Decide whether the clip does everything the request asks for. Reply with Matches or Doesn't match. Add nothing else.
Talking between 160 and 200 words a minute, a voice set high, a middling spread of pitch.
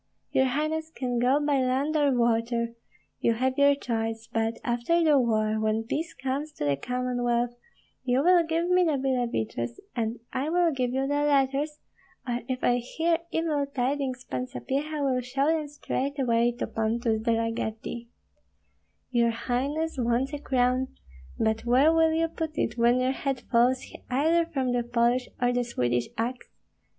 Matches